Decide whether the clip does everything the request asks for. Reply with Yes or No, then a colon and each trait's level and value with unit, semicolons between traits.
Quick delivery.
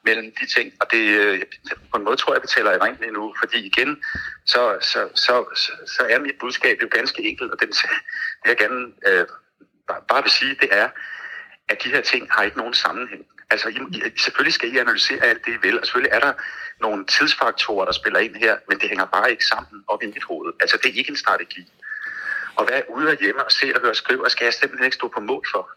Yes: fast, 240 wpm